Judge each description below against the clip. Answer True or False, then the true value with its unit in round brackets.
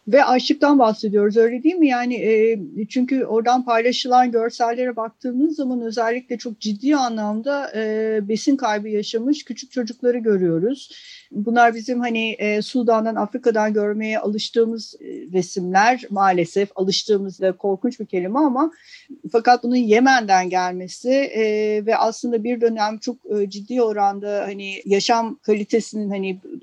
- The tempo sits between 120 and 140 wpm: True (135 wpm)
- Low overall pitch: False (230 Hz)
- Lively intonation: False (3.0 semitones)